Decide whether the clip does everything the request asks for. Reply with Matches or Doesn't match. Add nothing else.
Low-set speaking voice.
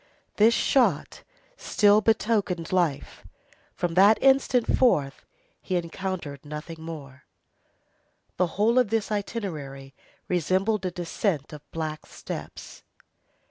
Doesn't match